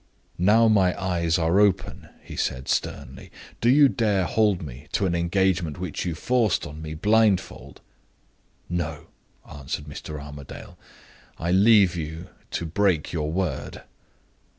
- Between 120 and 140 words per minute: Yes, slow, 135 wpm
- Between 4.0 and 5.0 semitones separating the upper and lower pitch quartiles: Yes, average, 4.4 semitones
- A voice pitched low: Yes, very low, 90 Hz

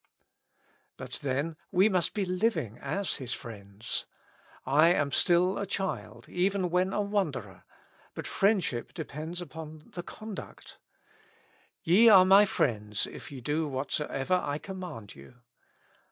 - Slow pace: Yes, slow, 130 wpm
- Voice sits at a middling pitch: Yes, medium, 165 Hz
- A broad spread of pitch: Yes, wide, 5.9 semitones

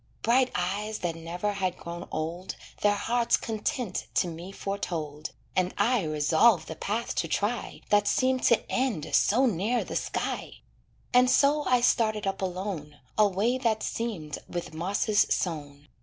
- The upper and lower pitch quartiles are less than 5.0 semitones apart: No, average, 5.3 semitones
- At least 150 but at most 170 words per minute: Yes, average, 155 wpm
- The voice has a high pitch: Yes, high, 200 Hz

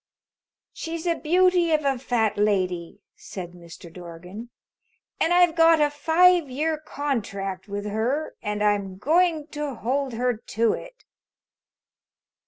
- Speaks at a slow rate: Yes, slow, 130 wpm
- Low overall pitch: No, very high, 255 Hz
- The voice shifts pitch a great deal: Yes, wide, 7.9 semitones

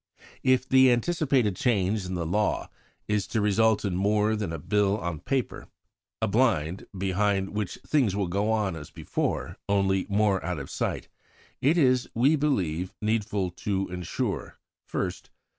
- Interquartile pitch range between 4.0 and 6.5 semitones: No, average, 3.4 semitones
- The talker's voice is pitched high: No, low, 105 Hz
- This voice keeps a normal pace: Yes, average, 155 wpm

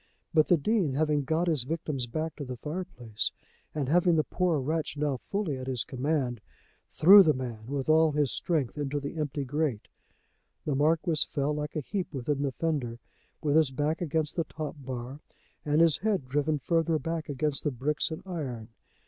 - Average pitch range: Yes, average, 3.1 semitones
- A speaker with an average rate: Yes, average, 185 wpm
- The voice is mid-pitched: Yes, medium, 150 Hz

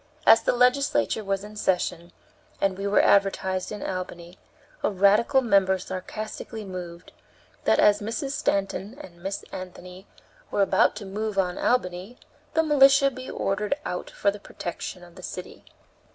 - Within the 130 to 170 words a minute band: Yes, average, 150 wpm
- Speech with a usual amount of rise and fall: Yes, average, 3.0 semitones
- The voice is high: Yes, high, 195 Hz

